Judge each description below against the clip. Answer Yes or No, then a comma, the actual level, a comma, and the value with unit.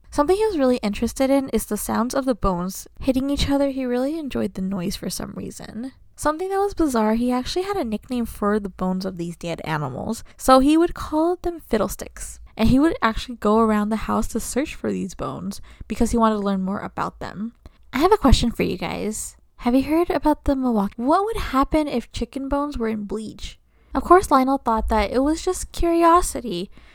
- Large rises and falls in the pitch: Yes, wide, 5.7 semitones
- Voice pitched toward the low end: No, high, 245 Hz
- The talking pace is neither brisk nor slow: No, fast, 215 wpm